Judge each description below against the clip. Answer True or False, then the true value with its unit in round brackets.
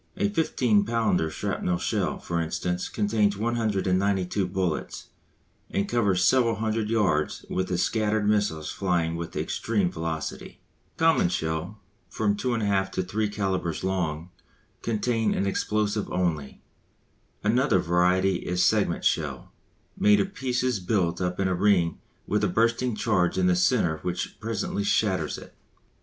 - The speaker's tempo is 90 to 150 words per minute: True (140 wpm)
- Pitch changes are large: False (3.5 semitones)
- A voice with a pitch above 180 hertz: False (95 Hz)